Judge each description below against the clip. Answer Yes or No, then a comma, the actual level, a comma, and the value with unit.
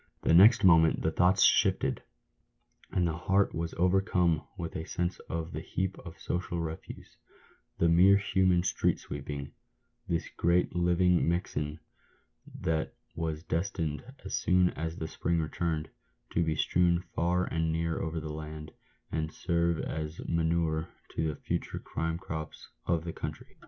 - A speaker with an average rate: Yes, average, 155 wpm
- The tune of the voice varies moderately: No, narrow, 1.8 semitones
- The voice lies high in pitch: No, very low, 85 Hz